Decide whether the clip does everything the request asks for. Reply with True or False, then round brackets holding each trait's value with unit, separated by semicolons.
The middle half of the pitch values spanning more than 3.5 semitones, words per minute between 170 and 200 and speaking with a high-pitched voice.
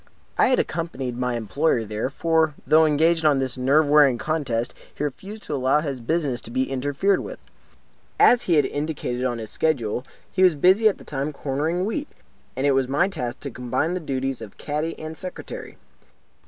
False (4.1 semitones; 190 wpm; 145 Hz)